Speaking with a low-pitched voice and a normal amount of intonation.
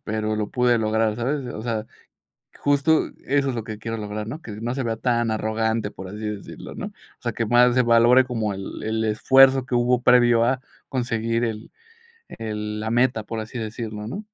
No: low, 115 Hz; narrow, 2.3 semitones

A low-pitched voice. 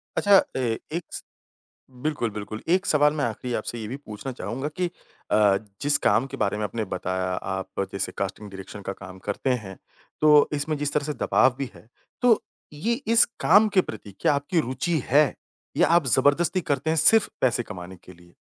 Yes: low, 130 Hz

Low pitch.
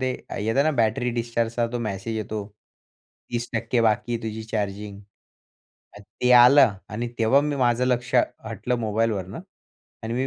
Yes: low, 115 Hz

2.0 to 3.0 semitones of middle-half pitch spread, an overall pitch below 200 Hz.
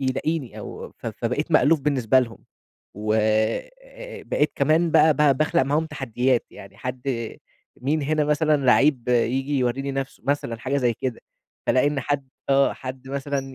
Yes: average, 2.7 semitones; low, 135 Hz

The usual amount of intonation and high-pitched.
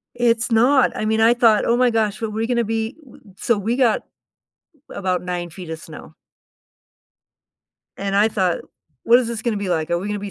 Yes: average, 3.1 semitones; high, 220 Hz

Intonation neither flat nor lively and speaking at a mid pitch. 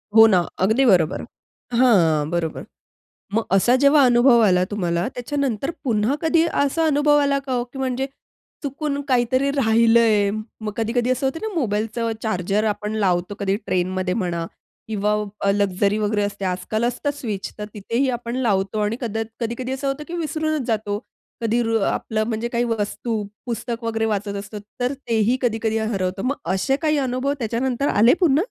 No: average, 4.1 semitones; high, 225 Hz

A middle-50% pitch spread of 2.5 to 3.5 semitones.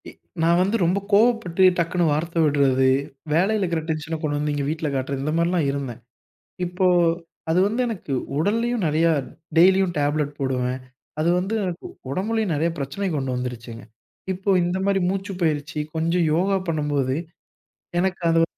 No: average, 4.4 semitones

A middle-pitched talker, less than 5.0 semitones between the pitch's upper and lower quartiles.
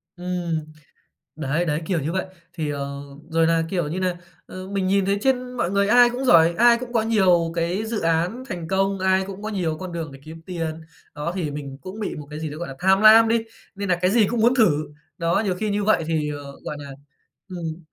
Yes: medium, 180 Hz; average, 4.0 semitones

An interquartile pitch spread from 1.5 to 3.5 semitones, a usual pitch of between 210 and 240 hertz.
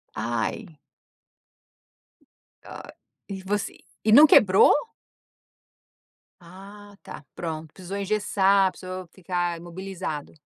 No: average, 2.7 semitones; high, 190 Hz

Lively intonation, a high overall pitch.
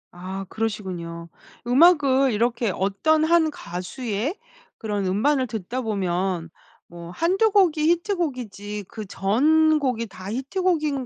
Yes: wide, 8.0 semitones; high, 235 Hz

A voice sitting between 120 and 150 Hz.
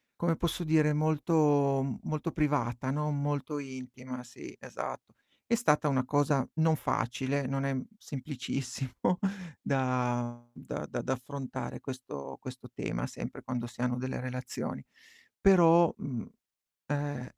Yes: low, 135 Hz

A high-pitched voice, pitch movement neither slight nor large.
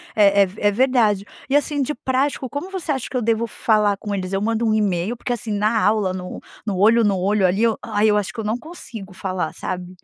Yes: high, 215 Hz; average, 3.3 semitones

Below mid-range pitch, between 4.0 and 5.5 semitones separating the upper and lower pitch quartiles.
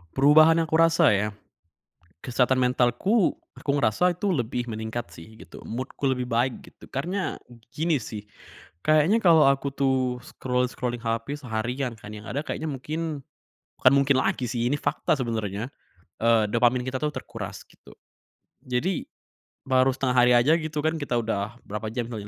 Yes: low, 130 Hz; average, 4.3 semitones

